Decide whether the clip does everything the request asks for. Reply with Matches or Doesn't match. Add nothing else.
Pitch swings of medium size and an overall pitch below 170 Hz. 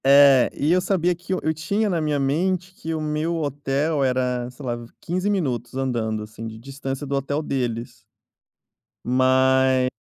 Matches